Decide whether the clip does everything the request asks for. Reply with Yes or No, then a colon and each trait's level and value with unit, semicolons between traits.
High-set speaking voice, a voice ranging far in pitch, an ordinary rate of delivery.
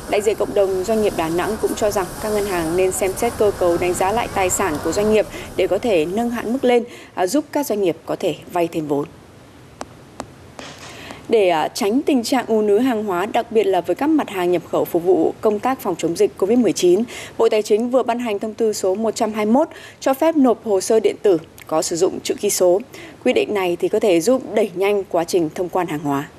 No: high, 210 Hz; average, 4.7 semitones; average, 240 wpm